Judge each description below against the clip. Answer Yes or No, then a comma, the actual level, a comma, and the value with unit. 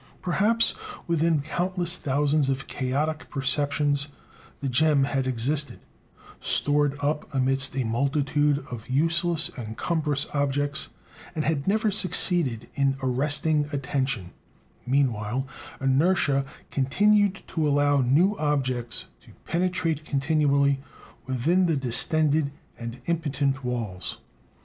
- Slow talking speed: Yes, slow, 105 wpm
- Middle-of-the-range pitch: Yes, medium, 145 Hz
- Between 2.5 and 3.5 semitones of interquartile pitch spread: Yes, average, 2.9 semitones